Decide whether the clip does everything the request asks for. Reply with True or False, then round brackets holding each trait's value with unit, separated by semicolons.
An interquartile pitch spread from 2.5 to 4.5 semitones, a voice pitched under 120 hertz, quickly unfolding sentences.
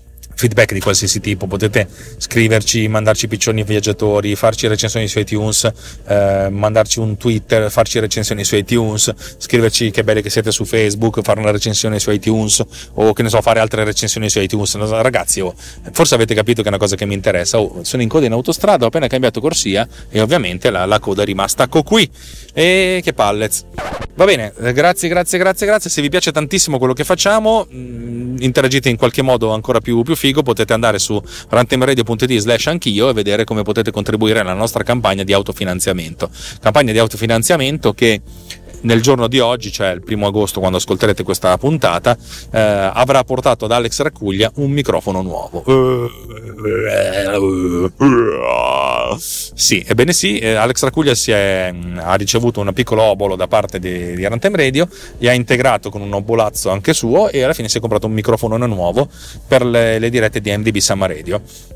True (3.3 semitones; 110 Hz; 175 wpm)